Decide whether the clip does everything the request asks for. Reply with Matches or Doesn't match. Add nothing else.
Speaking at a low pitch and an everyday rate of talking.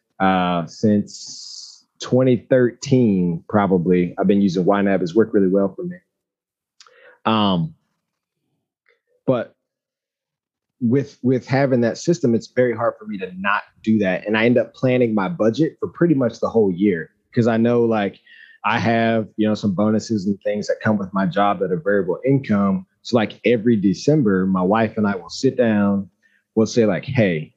Matches